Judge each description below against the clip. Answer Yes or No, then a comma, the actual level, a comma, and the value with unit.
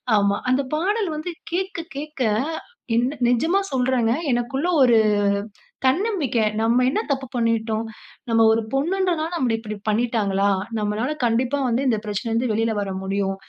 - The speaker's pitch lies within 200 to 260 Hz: Yes, high, 240 Hz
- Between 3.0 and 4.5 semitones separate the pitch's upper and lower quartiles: No, average, 5.1 semitones